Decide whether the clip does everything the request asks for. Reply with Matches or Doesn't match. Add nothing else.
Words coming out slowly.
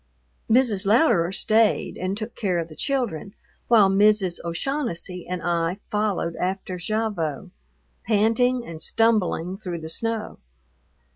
Matches